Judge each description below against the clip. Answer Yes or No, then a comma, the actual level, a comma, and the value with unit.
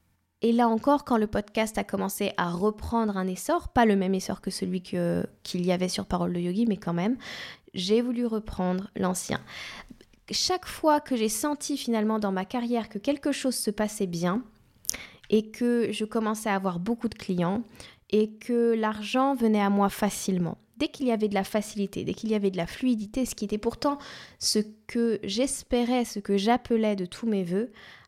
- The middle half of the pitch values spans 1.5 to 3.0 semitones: No, average, 3.4 semitones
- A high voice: Yes, high, 215 Hz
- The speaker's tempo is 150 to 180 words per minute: No, average, 195 wpm